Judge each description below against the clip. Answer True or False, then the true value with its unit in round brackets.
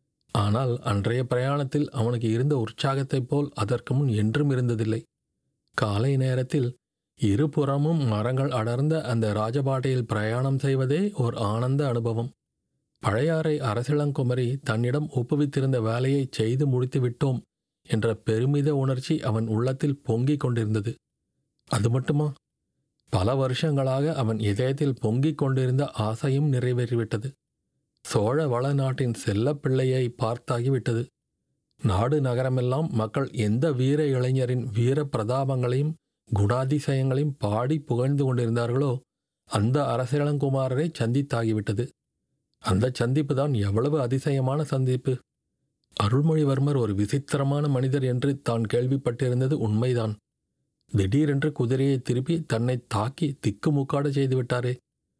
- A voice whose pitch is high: False (130 Hz)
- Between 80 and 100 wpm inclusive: True (95 wpm)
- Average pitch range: True (3.2 semitones)